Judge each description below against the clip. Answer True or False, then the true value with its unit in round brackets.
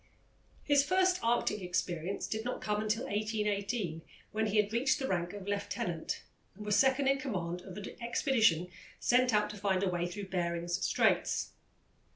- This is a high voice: True (210 Hz)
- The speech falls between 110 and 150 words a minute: False (170 wpm)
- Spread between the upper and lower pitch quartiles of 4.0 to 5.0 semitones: True (4.6 semitones)